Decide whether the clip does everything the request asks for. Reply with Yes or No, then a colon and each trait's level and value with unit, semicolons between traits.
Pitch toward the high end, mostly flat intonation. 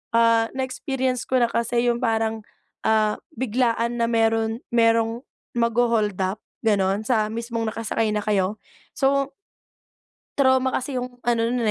Yes: high, 230 Hz; narrow, 1.8 semitones